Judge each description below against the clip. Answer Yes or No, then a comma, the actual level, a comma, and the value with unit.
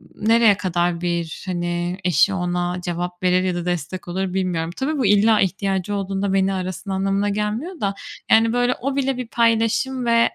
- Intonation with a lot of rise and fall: No, average, 4.0 semitones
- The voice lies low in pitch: No, high, 195 Hz